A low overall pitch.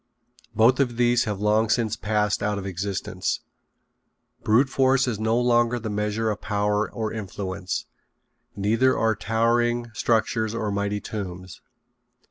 Yes: low, 110 Hz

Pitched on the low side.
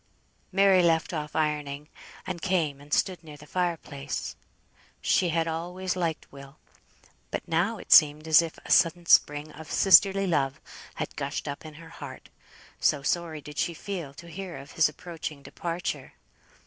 No: medium, 160 Hz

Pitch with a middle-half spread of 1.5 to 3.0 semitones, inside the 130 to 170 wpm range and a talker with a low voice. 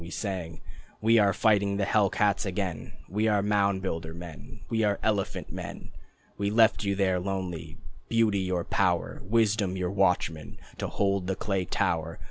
Yes: narrow, 2.4 semitones; average, 165 wpm; low, 100 Hz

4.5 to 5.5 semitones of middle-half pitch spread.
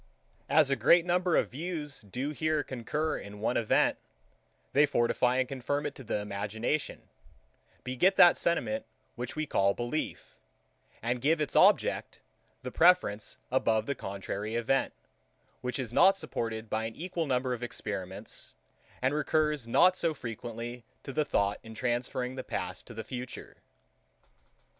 Yes: average, 5.2 semitones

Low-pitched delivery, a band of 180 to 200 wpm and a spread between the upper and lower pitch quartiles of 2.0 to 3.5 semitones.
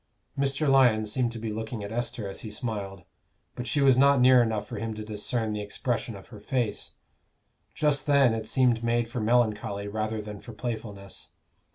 Yes: low, 115 Hz; average, 190 wpm; average, 2.7 semitones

